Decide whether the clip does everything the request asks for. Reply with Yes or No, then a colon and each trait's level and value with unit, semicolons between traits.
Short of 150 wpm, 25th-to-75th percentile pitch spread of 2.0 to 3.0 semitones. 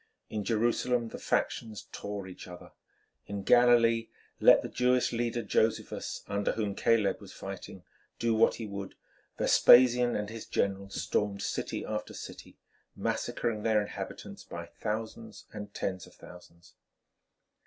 Yes: slow, 135 wpm; narrow, 2.5 semitones